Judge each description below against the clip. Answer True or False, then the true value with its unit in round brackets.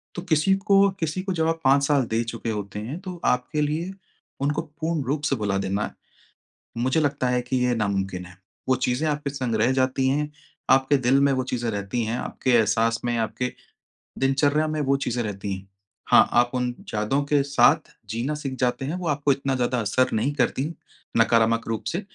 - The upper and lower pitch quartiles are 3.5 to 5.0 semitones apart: True (4.2 semitones)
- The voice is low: True (130 Hz)